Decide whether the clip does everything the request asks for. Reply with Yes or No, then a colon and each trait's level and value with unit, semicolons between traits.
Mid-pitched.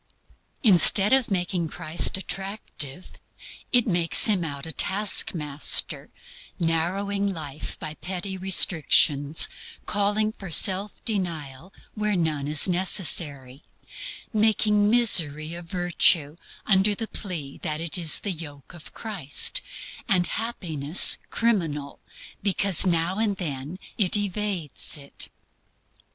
Yes: medium, 180 Hz